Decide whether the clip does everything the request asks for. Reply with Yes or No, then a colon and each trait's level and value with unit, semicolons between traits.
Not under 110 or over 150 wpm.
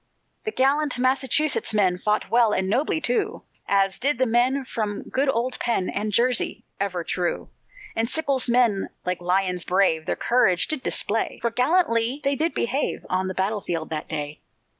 No: average, 170 wpm